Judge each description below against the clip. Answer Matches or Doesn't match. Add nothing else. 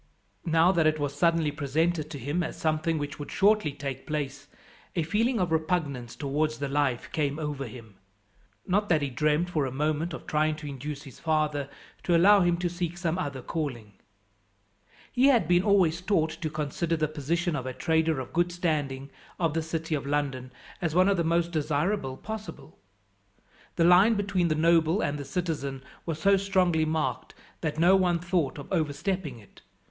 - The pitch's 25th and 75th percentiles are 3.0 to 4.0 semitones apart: Matches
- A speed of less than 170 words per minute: Doesn't match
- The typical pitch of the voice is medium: Matches